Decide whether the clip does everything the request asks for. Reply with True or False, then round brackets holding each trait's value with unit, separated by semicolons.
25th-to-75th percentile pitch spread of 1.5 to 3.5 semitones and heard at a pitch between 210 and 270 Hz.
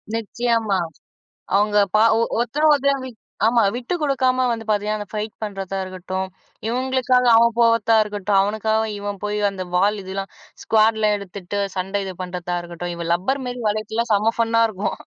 True (3.1 semitones; 215 Hz)